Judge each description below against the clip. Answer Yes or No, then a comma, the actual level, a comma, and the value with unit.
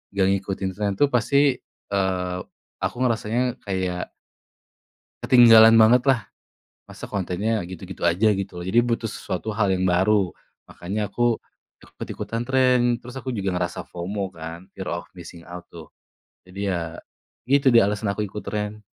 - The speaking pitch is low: Yes, low, 100 Hz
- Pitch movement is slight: No, average, 4.0 semitones